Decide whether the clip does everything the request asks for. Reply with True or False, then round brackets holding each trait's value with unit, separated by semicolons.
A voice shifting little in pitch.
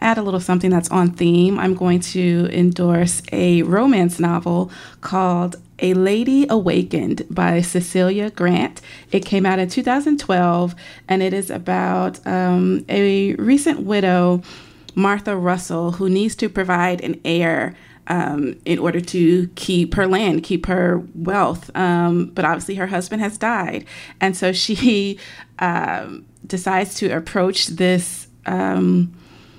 True (1.9 semitones)